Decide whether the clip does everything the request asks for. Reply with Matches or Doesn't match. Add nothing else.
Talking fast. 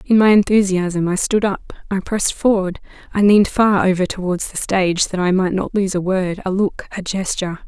Matches